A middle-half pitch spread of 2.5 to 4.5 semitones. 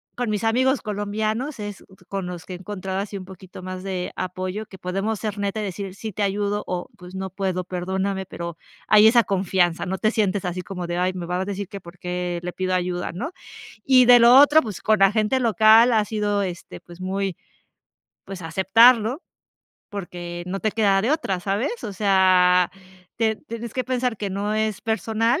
Yes: average, 3.0 semitones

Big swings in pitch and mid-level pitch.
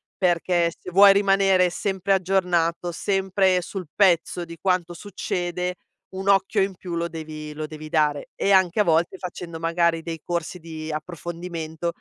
No: narrow, 2.4 semitones; medium, 175 Hz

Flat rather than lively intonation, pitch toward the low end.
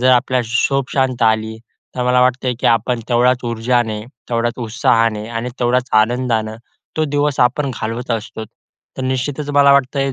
Yes: narrow, 2.3 semitones; low, 125 Hz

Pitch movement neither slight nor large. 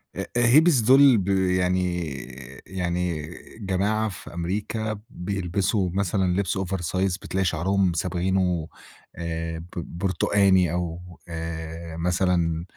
No: narrow, 2.3 semitones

